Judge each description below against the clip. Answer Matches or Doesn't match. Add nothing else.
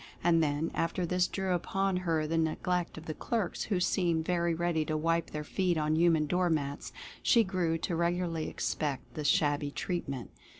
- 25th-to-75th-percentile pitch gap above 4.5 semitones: Doesn't match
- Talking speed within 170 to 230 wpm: Matches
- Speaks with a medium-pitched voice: Matches